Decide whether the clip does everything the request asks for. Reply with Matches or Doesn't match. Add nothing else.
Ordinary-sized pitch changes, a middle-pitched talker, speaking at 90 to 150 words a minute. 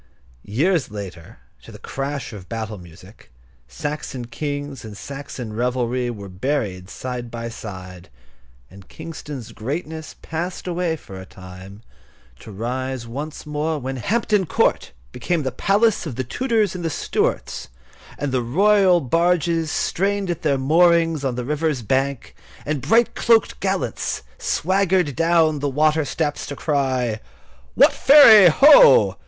Doesn't match